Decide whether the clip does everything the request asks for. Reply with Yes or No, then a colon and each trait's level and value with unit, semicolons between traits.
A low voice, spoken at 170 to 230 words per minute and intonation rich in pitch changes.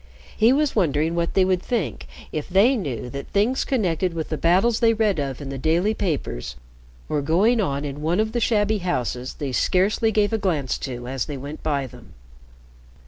No: medium, 170 Hz; average, 195 wpm; wide, 7.1 semitones